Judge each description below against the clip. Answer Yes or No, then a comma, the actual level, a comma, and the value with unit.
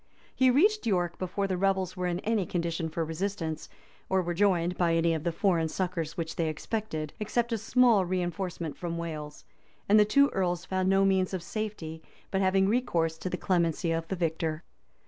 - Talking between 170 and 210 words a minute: Yes, average, 195 wpm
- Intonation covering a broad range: No, average, 2.9 semitones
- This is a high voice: No, medium, 180 Hz